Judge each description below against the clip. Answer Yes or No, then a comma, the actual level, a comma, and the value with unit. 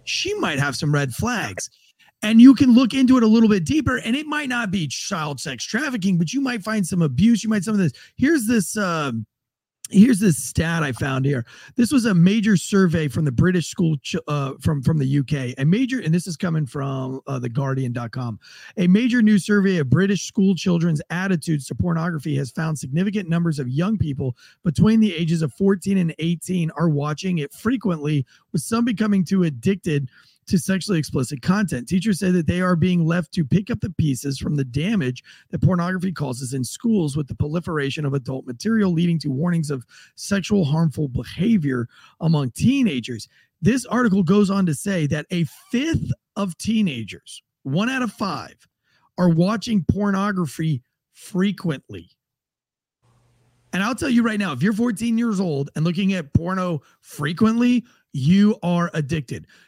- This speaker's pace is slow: No, average, 180 wpm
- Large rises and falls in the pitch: Yes, wide, 6.0 semitones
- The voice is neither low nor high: Yes, medium, 175 Hz